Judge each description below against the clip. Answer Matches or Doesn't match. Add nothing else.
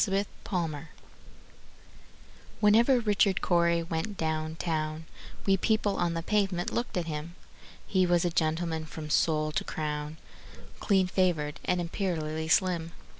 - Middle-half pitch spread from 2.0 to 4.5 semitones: Matches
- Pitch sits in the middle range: Matches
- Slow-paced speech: Matches